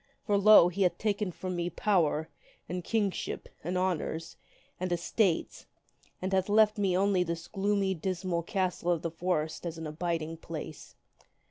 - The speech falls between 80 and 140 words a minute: No, average, 155 wpm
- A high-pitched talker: No, medium, 180 Hz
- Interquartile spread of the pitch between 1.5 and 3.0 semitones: Yes, average, 2.7 semitones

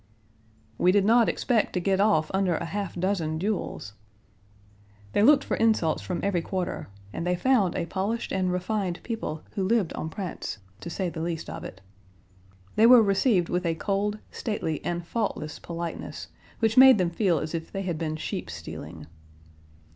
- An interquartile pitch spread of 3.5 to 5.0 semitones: Yes, average, 4.0 semitones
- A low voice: No, medium, 185 Hz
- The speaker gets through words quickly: No, average, 175 wpm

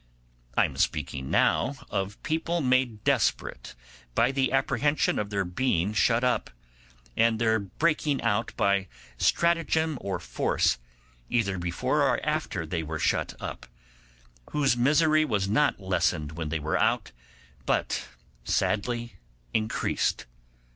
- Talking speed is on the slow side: Yes, slow, 125 wpm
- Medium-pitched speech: No, low, 110 Hz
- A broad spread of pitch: Yes, wide, 6.2 semitones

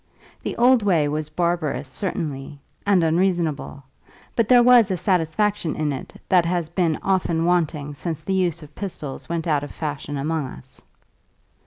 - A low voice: No, medium, 165 Hz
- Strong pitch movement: No, average, 3.8 semitones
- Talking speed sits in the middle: Yes, average, 160 wpm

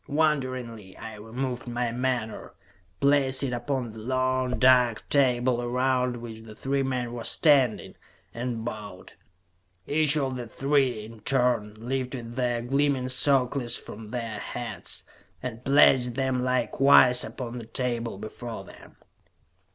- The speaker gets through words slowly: Yes, slow, 130 wpm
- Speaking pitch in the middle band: No, low, 125 Hz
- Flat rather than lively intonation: Yes, narrow, 2.1 semitones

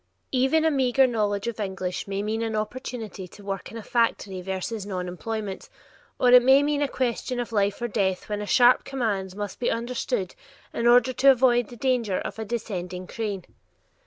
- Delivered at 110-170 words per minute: No, average, 190 wpm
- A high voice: Yes, high, 225 Hz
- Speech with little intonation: No, average, 3.8 semitones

